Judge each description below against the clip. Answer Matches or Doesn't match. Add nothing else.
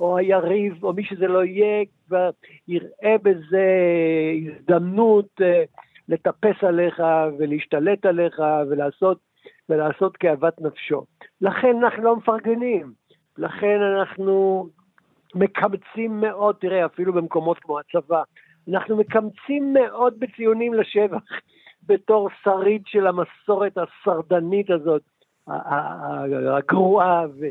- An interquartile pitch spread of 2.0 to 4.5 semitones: Matches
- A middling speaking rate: Doesn't match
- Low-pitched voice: Doesn't match